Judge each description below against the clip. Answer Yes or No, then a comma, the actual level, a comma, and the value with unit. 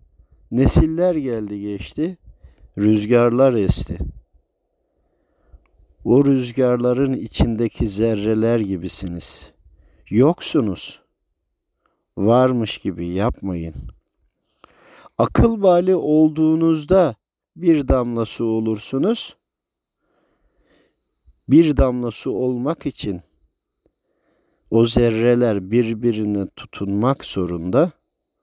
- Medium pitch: No, low, 115 Hz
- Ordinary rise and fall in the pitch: No, wide, 5.7 semitones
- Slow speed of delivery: Yes, slow, 65 wpm